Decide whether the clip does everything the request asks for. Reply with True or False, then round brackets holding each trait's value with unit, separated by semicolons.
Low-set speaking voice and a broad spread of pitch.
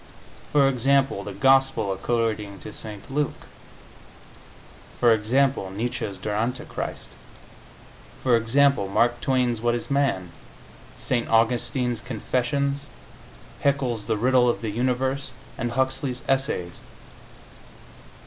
False (120 Hz; 3.4 semitones)